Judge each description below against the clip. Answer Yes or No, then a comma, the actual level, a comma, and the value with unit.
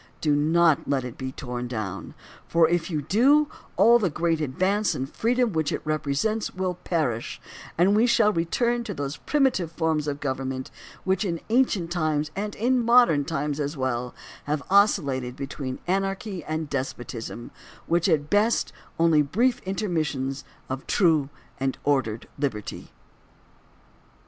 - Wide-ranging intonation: Yes, wide, 6.3 semitones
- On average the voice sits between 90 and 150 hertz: No, medium, 160 Hz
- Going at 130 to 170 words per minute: Yes, average, 150 wpm